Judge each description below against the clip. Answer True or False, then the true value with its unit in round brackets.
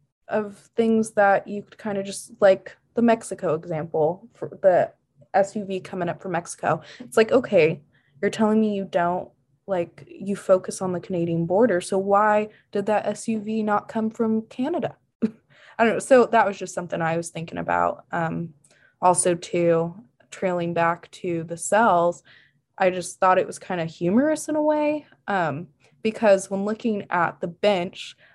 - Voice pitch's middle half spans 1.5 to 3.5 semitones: False (4.2 semitones)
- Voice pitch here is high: True (195 Hz)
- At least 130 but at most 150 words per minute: False (170 wpm)